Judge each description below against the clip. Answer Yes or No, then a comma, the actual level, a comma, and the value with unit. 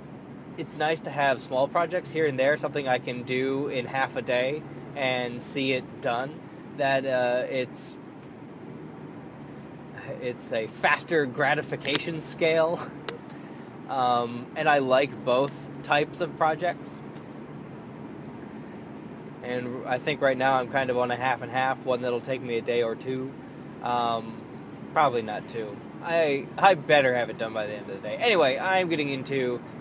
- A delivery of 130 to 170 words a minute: Yes, average, 155 wpm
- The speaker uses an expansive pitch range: No, average, 3.2 semitones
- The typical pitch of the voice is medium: No, low, 130 Hz